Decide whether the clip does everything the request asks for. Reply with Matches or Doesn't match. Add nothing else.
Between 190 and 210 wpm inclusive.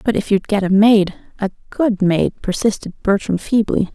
Doesn't match